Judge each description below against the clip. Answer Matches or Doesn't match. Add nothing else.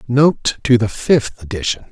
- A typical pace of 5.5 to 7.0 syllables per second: Doesn't match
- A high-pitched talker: Doesn't match